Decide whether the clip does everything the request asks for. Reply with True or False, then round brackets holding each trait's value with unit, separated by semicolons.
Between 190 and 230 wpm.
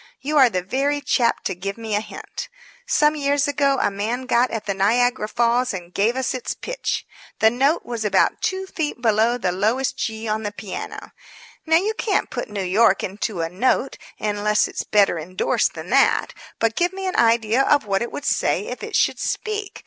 True (200 wpm)